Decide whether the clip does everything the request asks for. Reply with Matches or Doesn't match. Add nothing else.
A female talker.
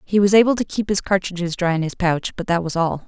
Matches